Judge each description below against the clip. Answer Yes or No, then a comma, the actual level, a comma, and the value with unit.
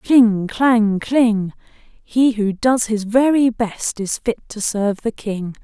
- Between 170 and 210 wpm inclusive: No, average, 160 wpm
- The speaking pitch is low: No, high, 220 Hz